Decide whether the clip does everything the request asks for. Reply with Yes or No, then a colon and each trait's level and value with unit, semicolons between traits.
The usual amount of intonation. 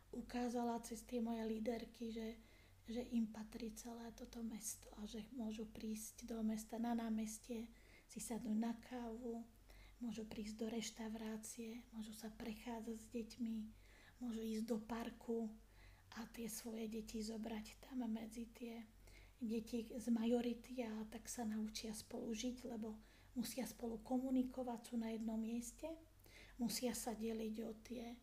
No: narrow, 1.1 semitones